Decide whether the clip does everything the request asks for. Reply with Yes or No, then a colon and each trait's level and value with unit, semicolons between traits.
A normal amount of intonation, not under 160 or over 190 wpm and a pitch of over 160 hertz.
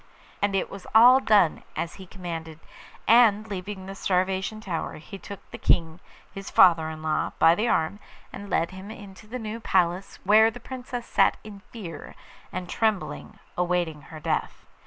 Yes: average, 4.0 semitones; average, 170 wpm; high, 190 Hz